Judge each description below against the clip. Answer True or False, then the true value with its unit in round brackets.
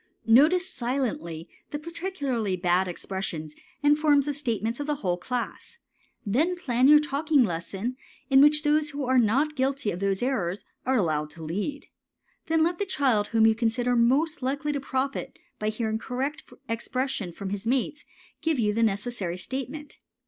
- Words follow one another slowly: False (165 wpm)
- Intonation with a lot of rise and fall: True (6.0 semitones)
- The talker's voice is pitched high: True (250 Hz)